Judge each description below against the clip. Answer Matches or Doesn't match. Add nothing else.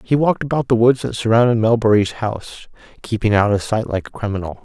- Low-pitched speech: Matches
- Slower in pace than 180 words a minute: Doesn't match